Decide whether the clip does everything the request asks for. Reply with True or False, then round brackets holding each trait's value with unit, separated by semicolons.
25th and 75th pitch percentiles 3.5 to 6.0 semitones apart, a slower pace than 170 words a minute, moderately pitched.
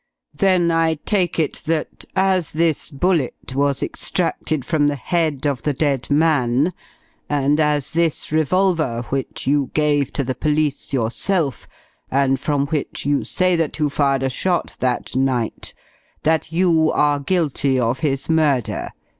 False (3.1 semitones; 145 wpm; 150 Hz)